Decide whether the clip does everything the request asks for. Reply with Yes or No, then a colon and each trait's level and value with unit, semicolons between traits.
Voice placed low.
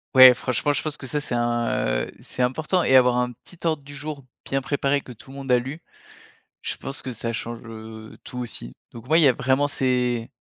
Yes: low, 130 Hz